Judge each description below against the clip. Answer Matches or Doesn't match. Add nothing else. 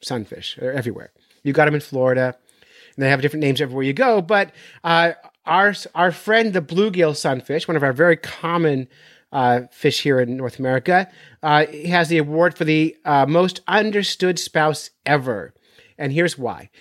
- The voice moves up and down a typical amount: Matches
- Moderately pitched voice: Matches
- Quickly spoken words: Doesn't match